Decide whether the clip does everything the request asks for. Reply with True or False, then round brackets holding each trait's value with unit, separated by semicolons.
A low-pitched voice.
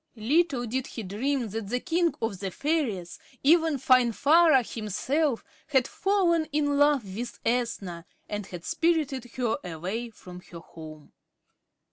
False (245 Hz)